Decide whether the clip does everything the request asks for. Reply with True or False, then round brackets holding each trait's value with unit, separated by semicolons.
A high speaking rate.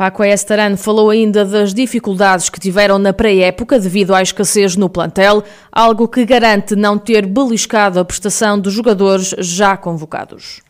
False (150 wpm)